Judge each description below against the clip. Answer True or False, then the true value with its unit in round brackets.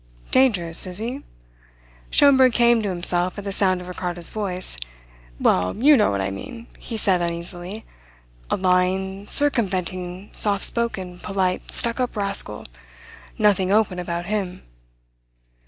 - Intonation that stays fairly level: False (3.4 semitones)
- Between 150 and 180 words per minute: False (135 wpm)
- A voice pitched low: False (190 Hz)